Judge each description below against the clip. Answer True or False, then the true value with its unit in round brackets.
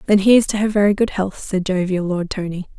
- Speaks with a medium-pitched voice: False (195 Hz)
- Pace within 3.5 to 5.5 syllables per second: False (5.9 syllables/s)